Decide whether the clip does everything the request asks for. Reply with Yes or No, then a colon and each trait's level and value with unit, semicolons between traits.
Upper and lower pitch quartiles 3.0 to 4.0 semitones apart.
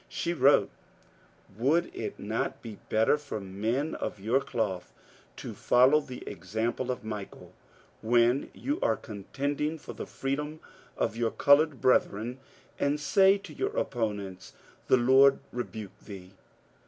No: average, 5.0 semitones